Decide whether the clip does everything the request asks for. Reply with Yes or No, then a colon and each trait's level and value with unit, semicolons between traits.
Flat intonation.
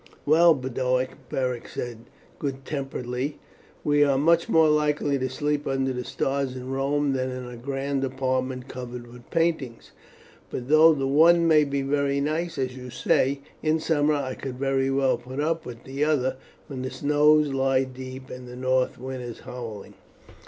Yes: narrow, 2.3 semitones